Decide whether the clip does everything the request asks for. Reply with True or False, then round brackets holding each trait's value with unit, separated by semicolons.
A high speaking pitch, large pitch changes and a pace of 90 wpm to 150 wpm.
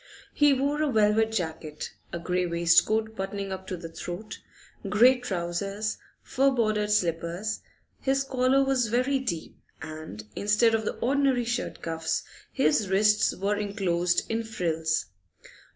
True (210 Hz; 5.7 semitones; 135 wpm)